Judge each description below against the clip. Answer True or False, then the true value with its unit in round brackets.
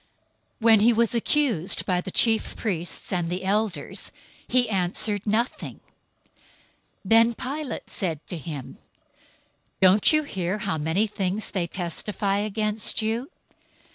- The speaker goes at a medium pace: False (130 wpm)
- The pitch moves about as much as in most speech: True (3.9 semitones)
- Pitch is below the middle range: False (205 Hz)